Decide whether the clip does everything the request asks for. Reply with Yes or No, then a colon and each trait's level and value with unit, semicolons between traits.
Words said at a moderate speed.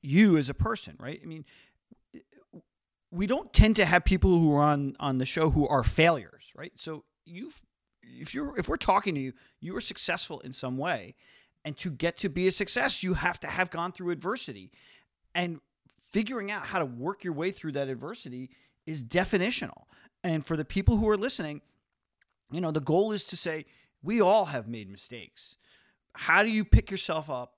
Yes: average, 195 wpm